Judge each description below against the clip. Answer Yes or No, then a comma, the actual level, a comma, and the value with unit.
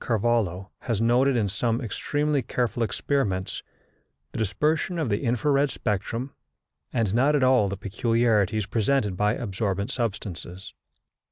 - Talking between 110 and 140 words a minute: Yes, slow, 135 wpm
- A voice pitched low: Yes, low, 115 Hz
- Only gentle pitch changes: No, average, 4.2 semitones